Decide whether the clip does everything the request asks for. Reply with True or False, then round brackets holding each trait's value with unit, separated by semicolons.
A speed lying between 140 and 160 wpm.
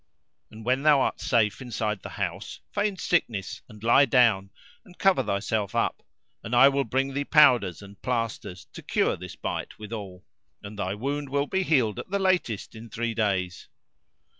False (175 wpm)